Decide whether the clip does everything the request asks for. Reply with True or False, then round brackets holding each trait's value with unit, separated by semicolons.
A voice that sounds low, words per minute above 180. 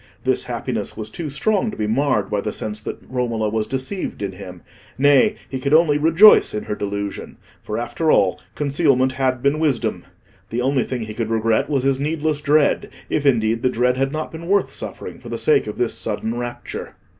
True (130 Hz; 200 wpm)